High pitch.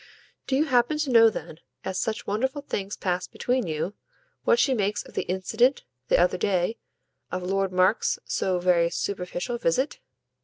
Yes: high, 200 Hz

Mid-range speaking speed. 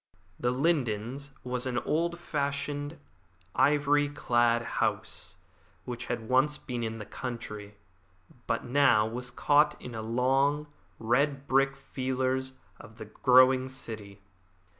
No: slow, 120 wpm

